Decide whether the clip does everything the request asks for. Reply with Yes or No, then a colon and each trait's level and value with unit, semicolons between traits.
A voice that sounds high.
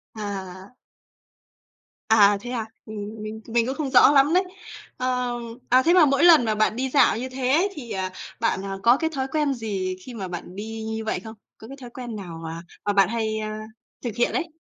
Yes: high, 225 Hz